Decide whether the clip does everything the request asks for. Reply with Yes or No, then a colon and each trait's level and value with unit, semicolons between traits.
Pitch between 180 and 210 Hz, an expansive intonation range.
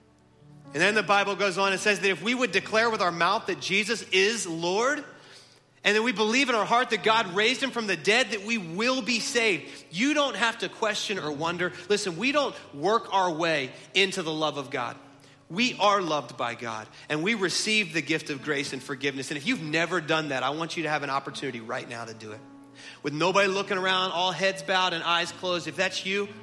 Yes: medium, 185 Hz; wide, 6.0 semitones